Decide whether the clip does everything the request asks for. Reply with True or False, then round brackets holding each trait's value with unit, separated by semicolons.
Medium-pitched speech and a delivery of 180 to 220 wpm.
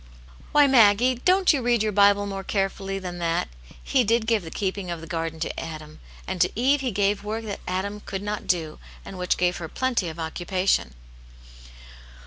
False (195 Hz; 195 wpm)